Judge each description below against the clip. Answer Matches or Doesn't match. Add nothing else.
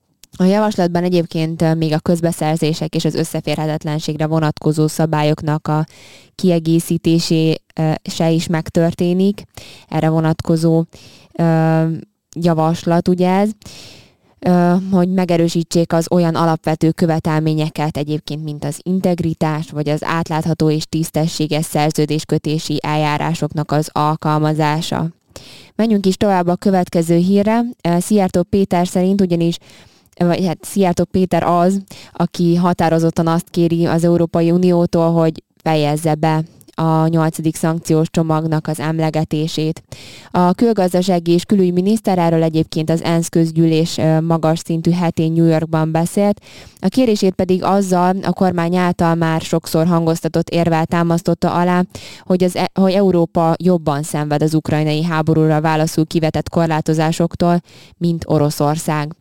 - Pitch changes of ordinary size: Doesn't match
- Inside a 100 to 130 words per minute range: Matches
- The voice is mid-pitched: Matches